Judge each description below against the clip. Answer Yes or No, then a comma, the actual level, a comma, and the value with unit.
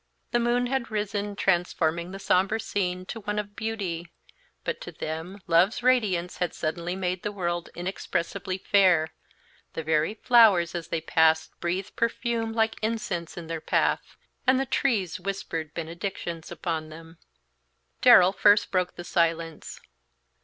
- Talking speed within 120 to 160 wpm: Yes, average, 145 wpm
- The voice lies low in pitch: No, medium, 185 Hz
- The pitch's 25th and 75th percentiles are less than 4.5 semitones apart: Yes, average, 3.9 semitones